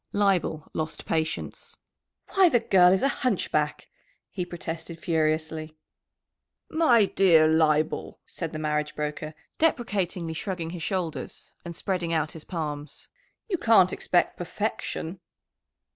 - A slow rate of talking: Yes, slow, 120 wpm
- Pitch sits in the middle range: Yes, medium, 170 Hz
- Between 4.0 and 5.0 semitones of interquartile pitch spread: No, average, 3.5 semitones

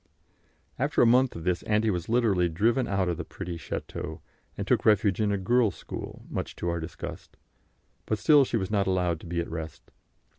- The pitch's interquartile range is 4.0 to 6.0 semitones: Yes, average, 4.6 semitones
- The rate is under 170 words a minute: No, average, 200 wpm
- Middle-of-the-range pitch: No, very low, 95 Hz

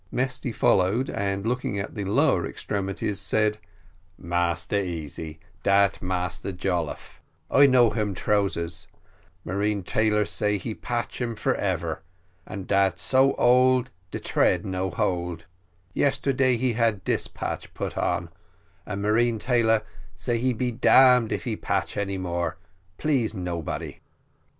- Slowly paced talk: Yes, slow, 130 wpm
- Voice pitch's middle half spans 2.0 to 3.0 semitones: No, average, 4.2 semitones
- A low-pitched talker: Yes, low, 100 Hz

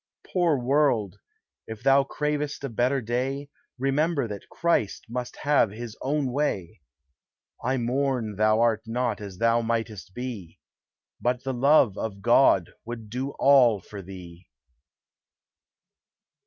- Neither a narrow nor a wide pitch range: Yes, average, 4.2 semitones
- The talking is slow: Yes, slow, 130 wpm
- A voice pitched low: Yes, low, 120 Hz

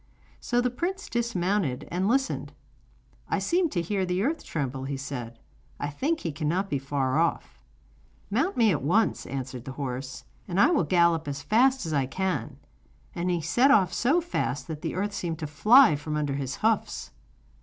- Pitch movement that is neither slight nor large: No, wide, 8.1 semitones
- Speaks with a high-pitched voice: No, medium, 175 Hz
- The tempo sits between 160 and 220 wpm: Yes, average, 185 wpm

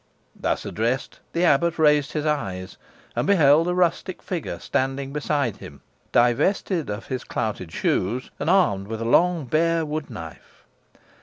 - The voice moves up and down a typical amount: No, wide, 6.4 semitones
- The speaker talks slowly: No, average, 150 wpm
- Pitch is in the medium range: Yes, medium, 145 Hz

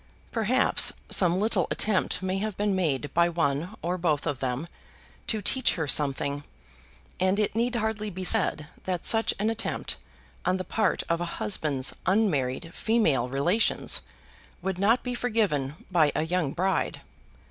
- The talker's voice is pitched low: No, medium, 185 Hz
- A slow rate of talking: No, average, 155 wpm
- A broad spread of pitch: Yes, wide, 5.8 semitones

